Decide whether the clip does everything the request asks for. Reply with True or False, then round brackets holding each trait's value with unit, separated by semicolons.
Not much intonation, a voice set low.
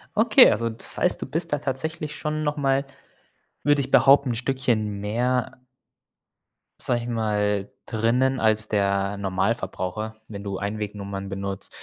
False (4.6 semitones; 110 Hz)